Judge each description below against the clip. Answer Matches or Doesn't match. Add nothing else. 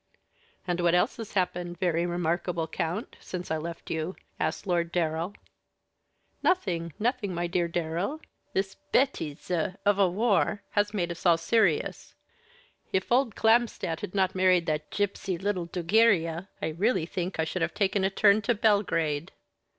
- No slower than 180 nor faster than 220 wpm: Doesn't match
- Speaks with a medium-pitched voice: Matches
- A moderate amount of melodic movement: Matches